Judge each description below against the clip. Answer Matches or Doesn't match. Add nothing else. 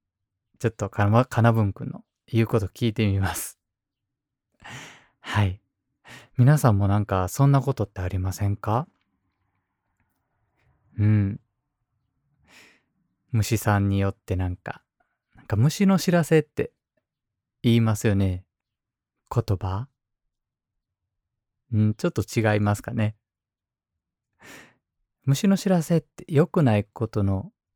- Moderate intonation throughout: Matches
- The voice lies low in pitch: Matches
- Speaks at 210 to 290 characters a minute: Matches